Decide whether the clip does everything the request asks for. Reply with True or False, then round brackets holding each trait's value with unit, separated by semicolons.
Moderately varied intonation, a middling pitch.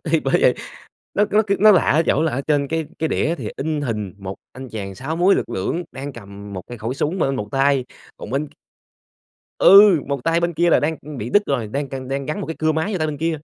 True (4.8 semitones; 145 Hz)